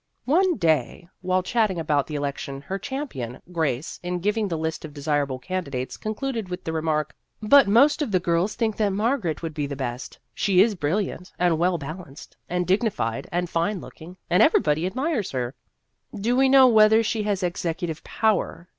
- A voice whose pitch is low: No, medium, 180 Hz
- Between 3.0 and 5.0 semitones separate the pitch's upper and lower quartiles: No, wide, 5.5 semitones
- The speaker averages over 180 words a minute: Yes, average, 190 wpm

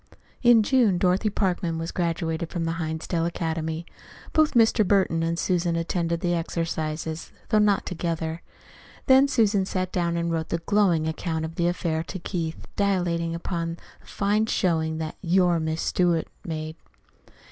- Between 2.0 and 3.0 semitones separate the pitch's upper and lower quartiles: Yes, narrow, 2.6 semitones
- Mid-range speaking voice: Yes, medium, 170 Hz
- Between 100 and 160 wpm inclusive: Yes, average, 155 wpm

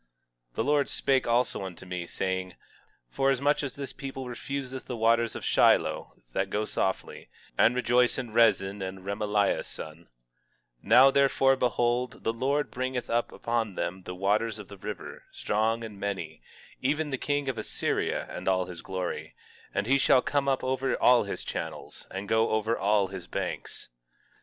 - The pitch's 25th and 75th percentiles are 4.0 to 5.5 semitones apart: Yes, average, 5.1 semitones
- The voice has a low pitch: Yes, low, 115 Hz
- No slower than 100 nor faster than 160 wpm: No, average, 175 wpm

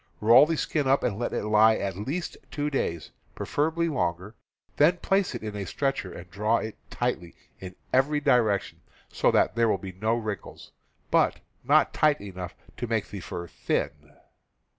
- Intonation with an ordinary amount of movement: No, wide, 6.5 semitones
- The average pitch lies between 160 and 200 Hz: No, low, 110 Hz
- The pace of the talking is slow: No, average, 180 wpm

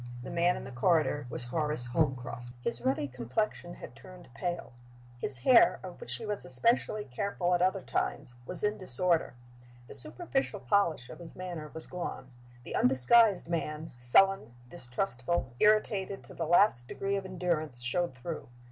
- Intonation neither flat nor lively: No, wide, 7.0 semitones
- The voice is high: No, medium, 170 Hz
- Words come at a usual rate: Yes, average, 160 wpm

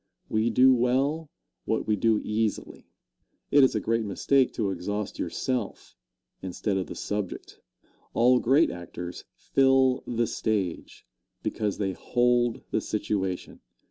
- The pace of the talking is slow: Yes, slow, 130 wpm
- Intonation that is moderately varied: Yes, average, 4.0 semitones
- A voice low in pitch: Yes, low, 110 Hz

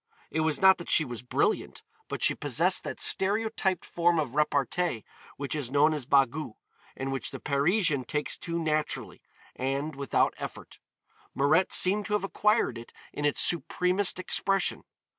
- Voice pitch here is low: No, medium, 155 Hz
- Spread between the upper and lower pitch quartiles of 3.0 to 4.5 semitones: No, average, 4.9 semitones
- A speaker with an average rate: Yes, average, 160 wpm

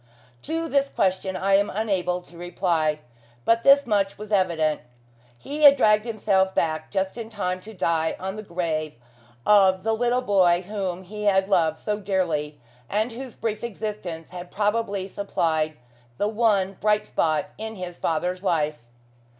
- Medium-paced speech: Yes, average, 160 wpm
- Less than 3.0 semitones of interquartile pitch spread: No, average, 3.4 semitones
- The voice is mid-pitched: No, high, 195 Hz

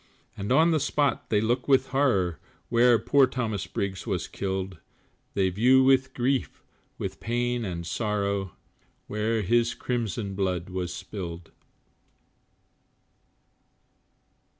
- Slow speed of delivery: Yes, slow, 115 wpm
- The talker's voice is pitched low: Yes, low, 110 Hz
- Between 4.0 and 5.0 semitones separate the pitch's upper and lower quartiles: Yes, average, 4.7 semitones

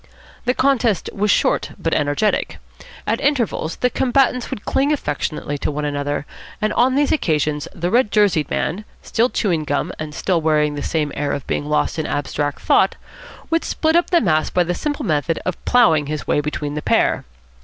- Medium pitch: Yes, medium, 165 Hz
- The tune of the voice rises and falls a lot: Yes, wide, 8.4 semitones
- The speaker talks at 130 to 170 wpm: No, average, 185 wpm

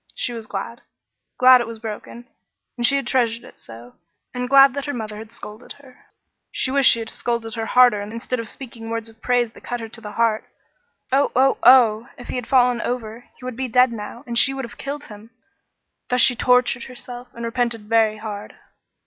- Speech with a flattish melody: Yes, narrow, 2.1 semitones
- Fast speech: Yes, fast, 210 wpm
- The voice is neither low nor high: No, high, 235 Hz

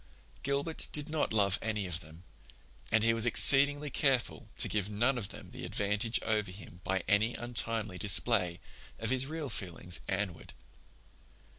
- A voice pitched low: Yes, low, 110 Hz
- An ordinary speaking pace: Yes, average, 160 wpm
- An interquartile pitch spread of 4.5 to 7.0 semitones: Yes, average, 5.1 semitones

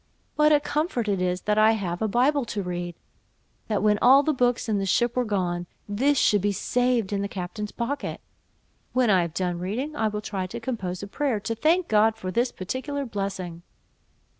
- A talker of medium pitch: No, high, 215 Hz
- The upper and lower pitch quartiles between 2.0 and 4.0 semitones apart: No, average, 4.7 semitones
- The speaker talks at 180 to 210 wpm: Yes, fast, 205 wpm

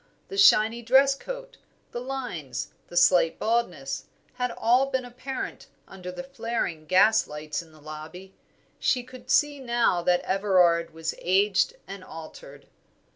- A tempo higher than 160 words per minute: No, slow, 135 wpm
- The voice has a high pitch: Yes, high, 195 Hz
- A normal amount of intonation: No, wide, 6.8 semitones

